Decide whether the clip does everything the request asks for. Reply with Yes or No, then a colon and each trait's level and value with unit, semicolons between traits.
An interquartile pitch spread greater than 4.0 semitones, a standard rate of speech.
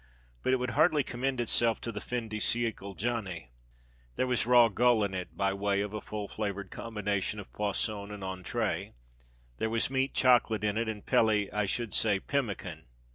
No: average, 3.1 semitones; average, 185 wpm